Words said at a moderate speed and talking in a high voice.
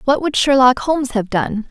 No: fast, 210 wpm; very high, 255 Hz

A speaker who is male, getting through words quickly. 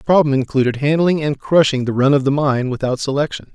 Yes: male; fast, 220 wpm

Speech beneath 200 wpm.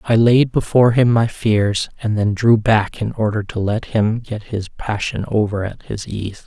No: fast, 205 wpm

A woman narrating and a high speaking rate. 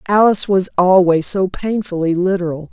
No: female; slow, 130 wpm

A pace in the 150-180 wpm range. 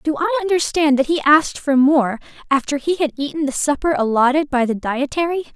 No: average, 195 wpm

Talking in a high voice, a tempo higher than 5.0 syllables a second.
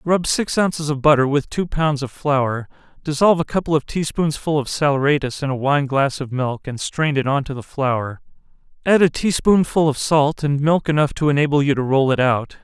No: medium, 145 Hz; 5.2 syllables/s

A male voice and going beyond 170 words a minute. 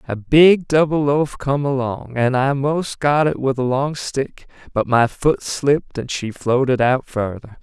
Yes: male; average, 190 wpm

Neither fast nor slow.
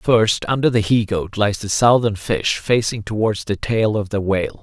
No: fast, 210 wpm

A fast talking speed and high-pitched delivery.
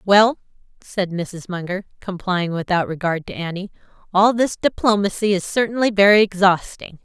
No: slow, 135 wpm; high, 195 Hz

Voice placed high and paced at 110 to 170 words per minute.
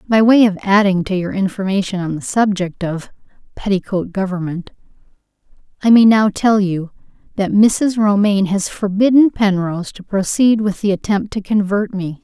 Yes: high, 200 Hz; average, 155 wpm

